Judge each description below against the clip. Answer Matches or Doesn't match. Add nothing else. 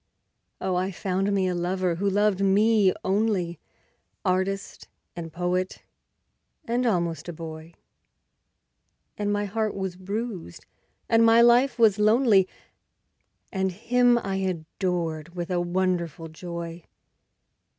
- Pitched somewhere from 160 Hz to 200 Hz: Matches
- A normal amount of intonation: Matches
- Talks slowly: Matches